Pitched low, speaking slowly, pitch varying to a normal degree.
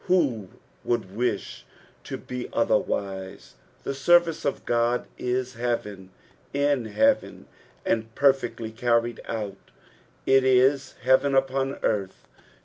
Yes: low, 125 Hz; slow, 115 wpm; average, 3.3 semitones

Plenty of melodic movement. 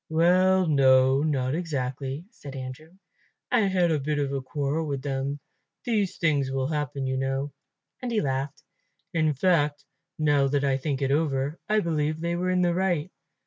No: average, 3.9 semitones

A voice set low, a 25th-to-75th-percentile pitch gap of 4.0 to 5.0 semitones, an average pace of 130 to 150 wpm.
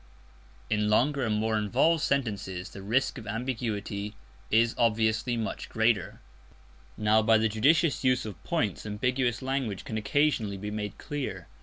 No: low, 110 Hz; average, 3.3 semitones; average, 145 wpm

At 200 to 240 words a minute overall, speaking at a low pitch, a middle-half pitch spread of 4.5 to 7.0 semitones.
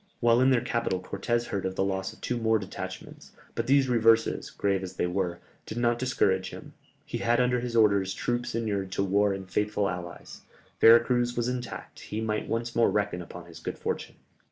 No: fast, 205 wpm; low, 110 Hz; average, 3.8 semitones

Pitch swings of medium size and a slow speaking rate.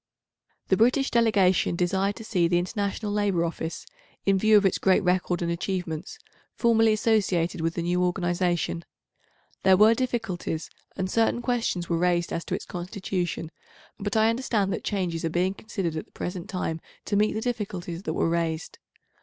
No: average, 3.6 semitones; average, 170 wpm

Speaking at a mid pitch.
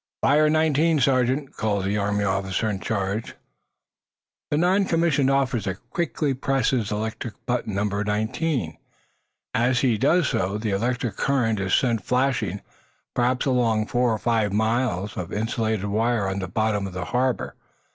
No: low, 115 Hz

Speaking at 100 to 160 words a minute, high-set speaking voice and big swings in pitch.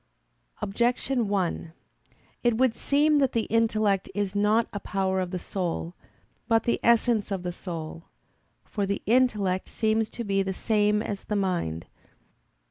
No: average, 150 wpm; high, 205 Hz; average, 3.2 semitones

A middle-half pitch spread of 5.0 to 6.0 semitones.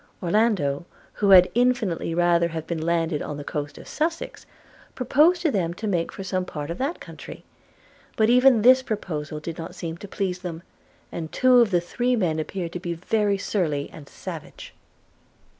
Yes: average, 5.3 semitones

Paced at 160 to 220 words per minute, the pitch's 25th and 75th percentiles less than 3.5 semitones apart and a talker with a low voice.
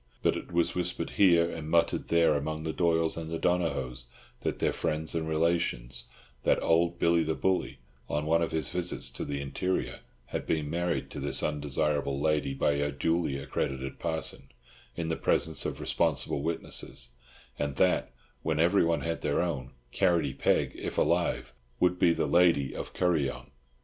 Yes: average, 170 wpm; average, 2.9 semitones; very low, 80 Hz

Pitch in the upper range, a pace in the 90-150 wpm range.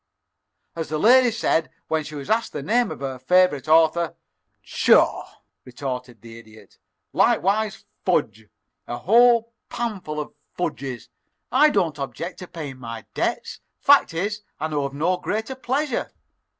No: medium, 160 Hz; average, 145 wpm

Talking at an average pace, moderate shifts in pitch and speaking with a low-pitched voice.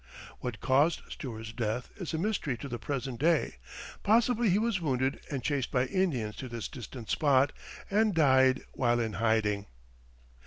No: average, 160 wpm; wide, 5.7 semitones; low, 130 Hz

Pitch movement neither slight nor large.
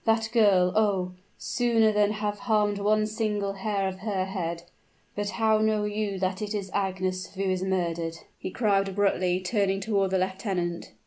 No: narrow, 2.2 semitones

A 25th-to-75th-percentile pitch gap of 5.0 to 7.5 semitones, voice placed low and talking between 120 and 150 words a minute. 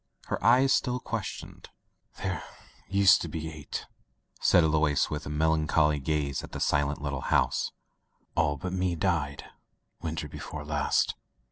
No: average, 3.8 semitones; very low, 80 Hz; average, 140 wpm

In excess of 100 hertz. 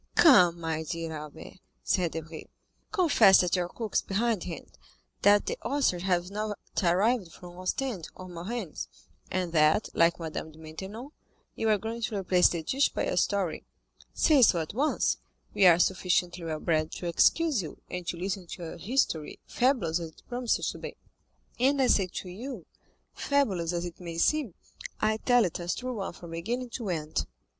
Yes: medium, 185 Hz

